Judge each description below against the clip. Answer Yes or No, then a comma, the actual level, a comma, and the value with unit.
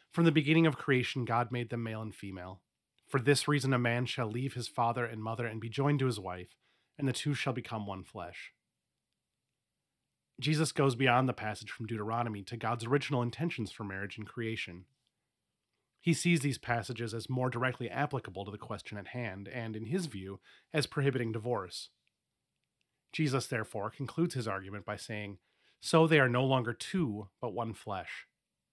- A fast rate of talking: No, average, 180 wpm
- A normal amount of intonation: Yes, average, 3.7 semitones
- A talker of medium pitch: No, low, 120 Hz